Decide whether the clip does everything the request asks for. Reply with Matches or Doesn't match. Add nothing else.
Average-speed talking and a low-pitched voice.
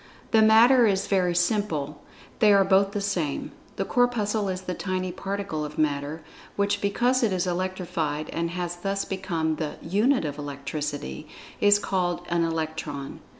Doesn't match